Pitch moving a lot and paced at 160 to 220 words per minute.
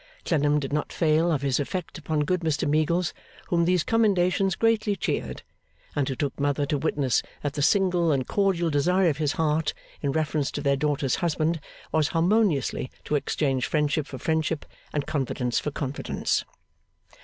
No: average, 3.2 semitones; average, 165 wpm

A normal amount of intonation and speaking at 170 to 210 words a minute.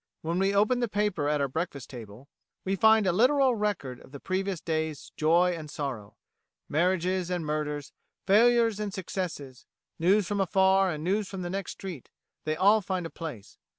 Yes: average, 4.6 semitones; average, 180 wpm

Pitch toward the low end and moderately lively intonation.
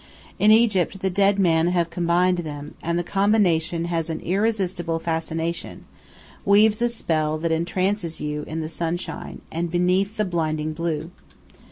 No: medium, 170 Hz; average, 3.1 semitones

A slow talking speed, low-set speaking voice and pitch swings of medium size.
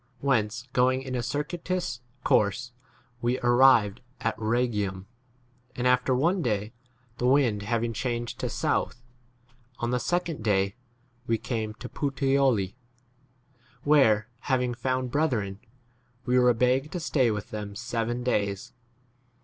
Yes: slow, 130 wpm; low, 120 Hz; average, 3.2 semitones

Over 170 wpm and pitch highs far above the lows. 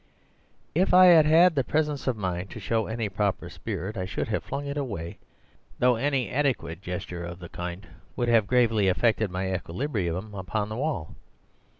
Yes: average, 180 wpm; wide, 6.6 semitones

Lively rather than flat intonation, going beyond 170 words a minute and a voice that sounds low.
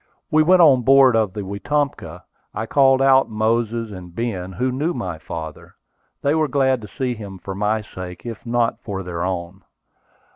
Yes: wide, 5.7 semitones; average, 180 wpm; low, 115 Hz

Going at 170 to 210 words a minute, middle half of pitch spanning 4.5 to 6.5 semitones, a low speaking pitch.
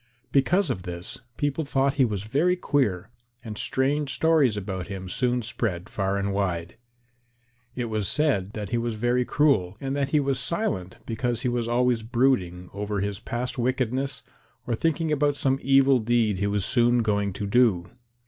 Yes: average, 175 wpm; average, 5.1 semitones; low, 120 Hz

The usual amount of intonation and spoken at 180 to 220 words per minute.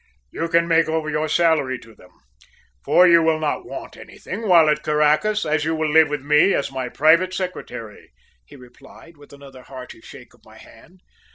Yes: average, 3.1 semitones; average, 190 wpm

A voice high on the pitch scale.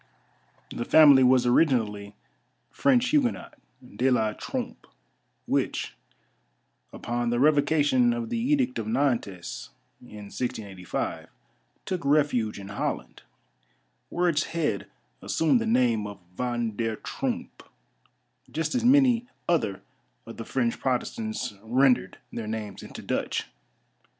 No: low, 130 Hz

